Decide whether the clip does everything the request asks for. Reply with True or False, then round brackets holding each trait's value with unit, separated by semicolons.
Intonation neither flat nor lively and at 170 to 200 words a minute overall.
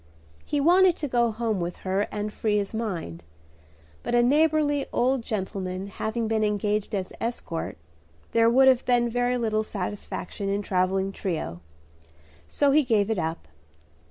False (4.0 semitones; 155 wpm)